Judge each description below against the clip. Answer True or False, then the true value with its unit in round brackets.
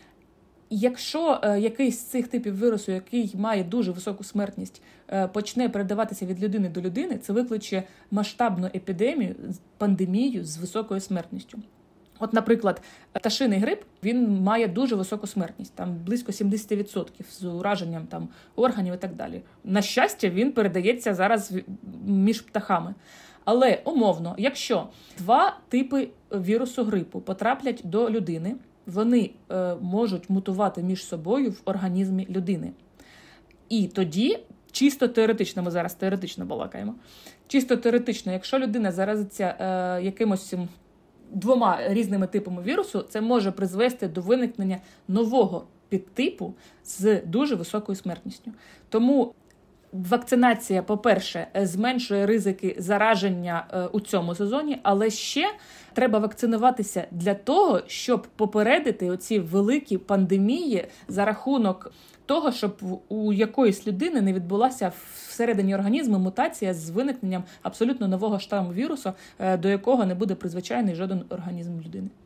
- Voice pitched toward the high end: True (205 Hz)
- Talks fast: False (120 wpm)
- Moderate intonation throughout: True (3.6 semitones)